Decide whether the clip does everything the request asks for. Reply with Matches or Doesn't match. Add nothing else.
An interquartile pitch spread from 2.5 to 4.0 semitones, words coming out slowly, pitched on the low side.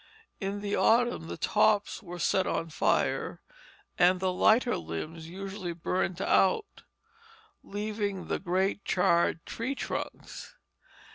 Doesn't match